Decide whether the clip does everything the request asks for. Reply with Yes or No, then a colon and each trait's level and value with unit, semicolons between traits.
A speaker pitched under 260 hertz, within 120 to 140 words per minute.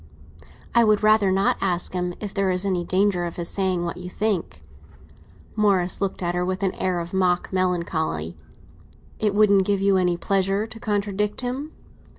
No: high, 190 Hz; average, 175 wpm